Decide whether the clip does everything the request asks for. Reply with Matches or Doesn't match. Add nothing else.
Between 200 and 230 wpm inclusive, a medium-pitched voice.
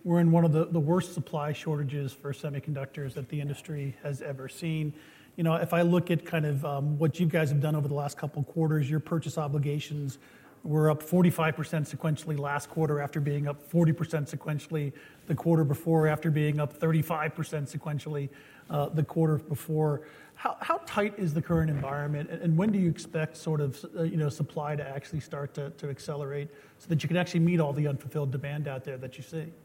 Matches